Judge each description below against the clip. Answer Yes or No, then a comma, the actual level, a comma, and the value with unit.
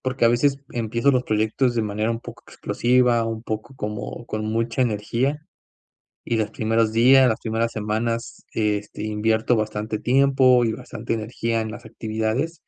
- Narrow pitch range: Yes, narrow, 2.0 semitones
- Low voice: Yes, low, 115 Hz